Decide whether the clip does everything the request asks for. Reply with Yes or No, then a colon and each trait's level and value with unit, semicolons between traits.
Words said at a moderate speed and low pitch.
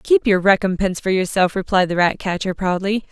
No: average, 175 wpm; high, 195 Hz